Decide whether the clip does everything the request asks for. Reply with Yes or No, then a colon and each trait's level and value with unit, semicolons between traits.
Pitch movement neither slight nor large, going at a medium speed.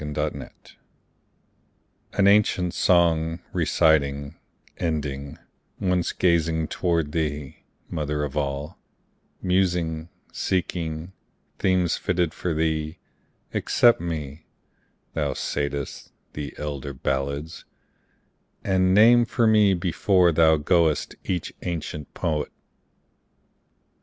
No: average, 3.3 semitones; slow, 90 wpm